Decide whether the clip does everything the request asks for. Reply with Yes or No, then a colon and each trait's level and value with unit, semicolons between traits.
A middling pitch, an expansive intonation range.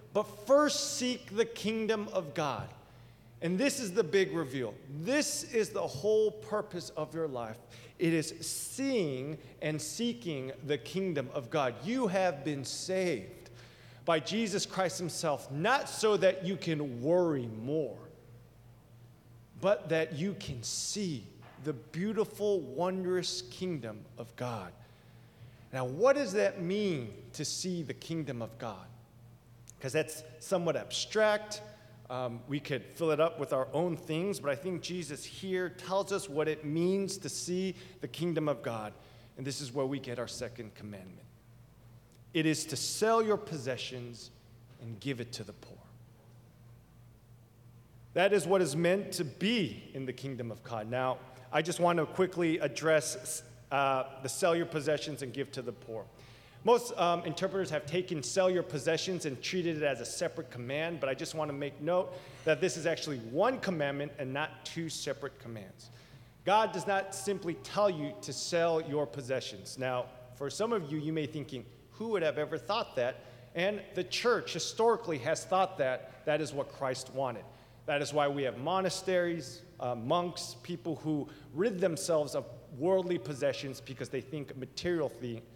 Yes: medium, 150 Hz; wide, 6.3 semitones